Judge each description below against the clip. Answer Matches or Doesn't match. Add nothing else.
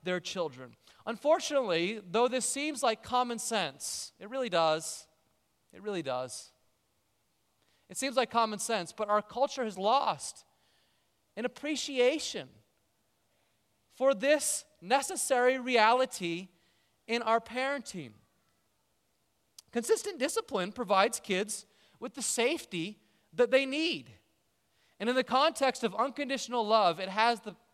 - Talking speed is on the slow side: Matches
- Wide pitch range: Matches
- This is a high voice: Matches